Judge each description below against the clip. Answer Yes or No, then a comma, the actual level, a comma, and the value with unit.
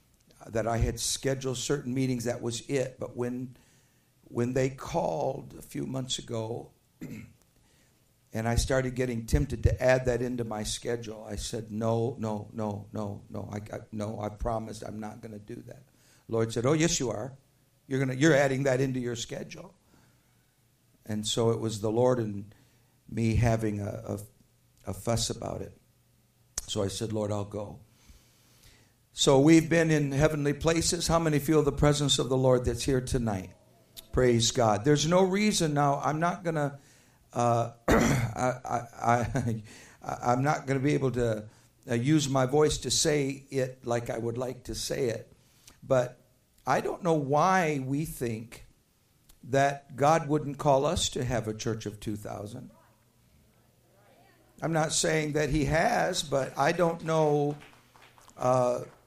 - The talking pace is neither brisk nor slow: Yes, average, 170 wpm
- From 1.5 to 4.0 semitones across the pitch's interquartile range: Yes, average, 3.7 semitones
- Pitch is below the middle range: Yes, low, 125 Hz